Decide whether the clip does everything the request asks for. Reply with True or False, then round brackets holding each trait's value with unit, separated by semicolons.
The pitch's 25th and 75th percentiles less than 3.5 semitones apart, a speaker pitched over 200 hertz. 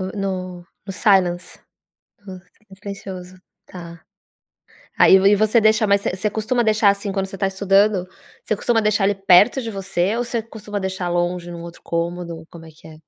False (2.8 semitones; 195 Hz)